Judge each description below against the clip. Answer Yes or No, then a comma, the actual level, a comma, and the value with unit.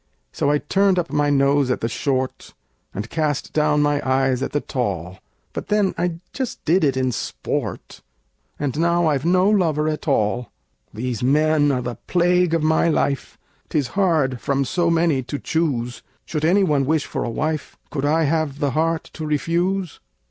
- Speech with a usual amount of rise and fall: Yes, average, 3.7 semitones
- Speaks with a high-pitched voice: No, medium, 150 Hz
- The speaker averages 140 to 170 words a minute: No, average, 180 wpm